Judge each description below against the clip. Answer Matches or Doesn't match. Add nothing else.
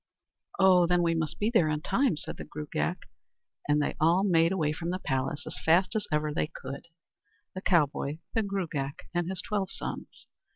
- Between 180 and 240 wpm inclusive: Matches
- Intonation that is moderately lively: Matches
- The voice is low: Doesn't match